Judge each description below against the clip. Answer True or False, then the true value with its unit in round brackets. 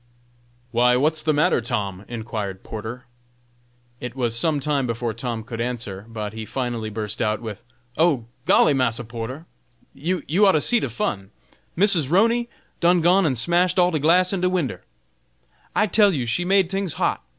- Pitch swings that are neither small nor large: False (7.4 semitones)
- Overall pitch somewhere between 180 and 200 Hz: False (130 Hz)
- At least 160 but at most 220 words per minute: True (175 wpm)